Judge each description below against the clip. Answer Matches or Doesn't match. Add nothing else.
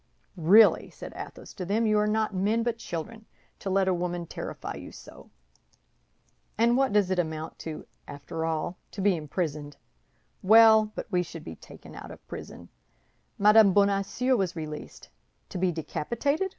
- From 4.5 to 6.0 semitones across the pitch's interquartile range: Matches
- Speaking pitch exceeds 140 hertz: Matches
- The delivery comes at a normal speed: Matches